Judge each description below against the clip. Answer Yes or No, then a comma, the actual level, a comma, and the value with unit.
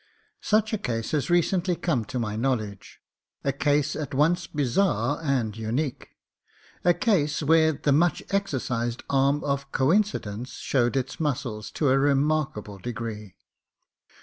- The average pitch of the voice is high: No, medium, 140 Hz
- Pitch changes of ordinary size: Yes, average, 4.8 semitones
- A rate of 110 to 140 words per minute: Yes, slow, 135 wpm